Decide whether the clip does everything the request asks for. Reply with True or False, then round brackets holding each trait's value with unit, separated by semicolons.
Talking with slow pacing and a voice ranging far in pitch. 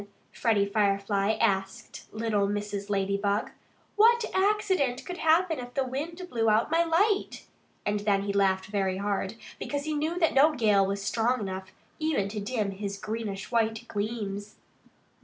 False (150 wpm; 6.5 semitones)